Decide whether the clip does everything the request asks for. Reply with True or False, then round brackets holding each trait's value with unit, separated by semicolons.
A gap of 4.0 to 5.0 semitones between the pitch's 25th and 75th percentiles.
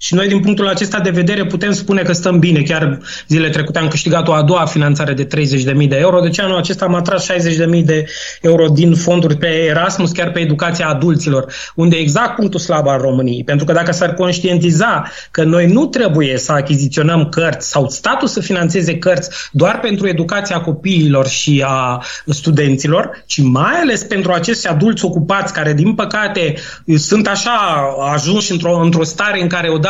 False (3.5 semitones)